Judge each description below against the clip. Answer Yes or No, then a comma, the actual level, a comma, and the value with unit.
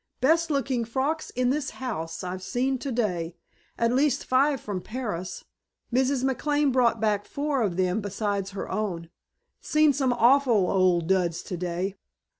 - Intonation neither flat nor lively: No, wide, 6.2 semitones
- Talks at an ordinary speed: Yes, average, 145 wpm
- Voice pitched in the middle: No, high, 230 Hz